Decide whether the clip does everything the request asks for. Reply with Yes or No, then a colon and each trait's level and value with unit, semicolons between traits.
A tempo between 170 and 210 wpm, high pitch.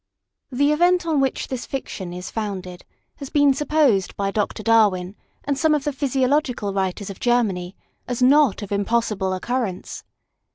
No: average, 155 wpm; high, 235 Hz